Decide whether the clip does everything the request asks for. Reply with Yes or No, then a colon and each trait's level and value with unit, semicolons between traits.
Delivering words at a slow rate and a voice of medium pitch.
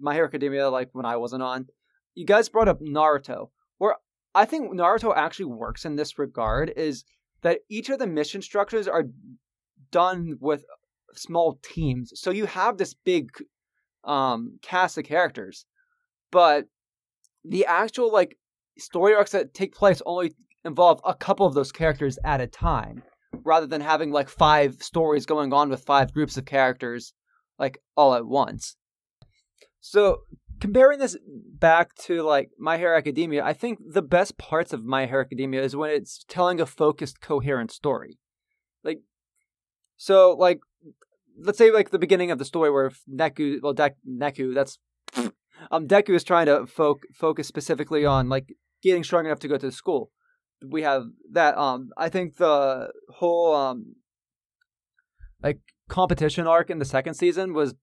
No: average, 160 wpm; medium, 160 Hz